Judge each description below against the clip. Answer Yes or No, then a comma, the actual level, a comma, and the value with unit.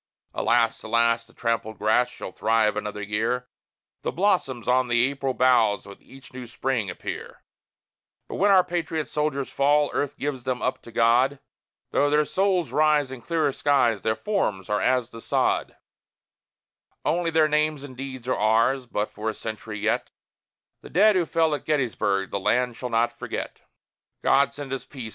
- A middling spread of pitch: Yes, average, 4.4 semitones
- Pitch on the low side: Yes, low, 130 Hz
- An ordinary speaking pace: Yes, average, 170 wpm